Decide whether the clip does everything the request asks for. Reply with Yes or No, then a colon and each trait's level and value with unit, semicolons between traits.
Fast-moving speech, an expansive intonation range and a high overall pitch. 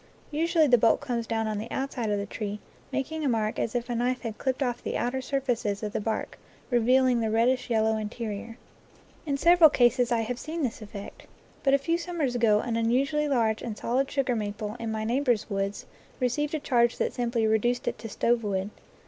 No: fast, 210 wpm; average, 3.2 semitones; high, 240 Hz